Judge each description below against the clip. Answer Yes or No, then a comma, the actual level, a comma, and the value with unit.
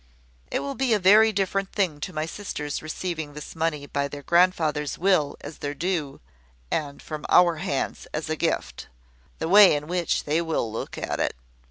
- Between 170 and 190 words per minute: Yes, average, 185 wpm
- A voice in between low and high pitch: Yes, medium, 160 Hz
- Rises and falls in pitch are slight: No, average, 3.9 semitones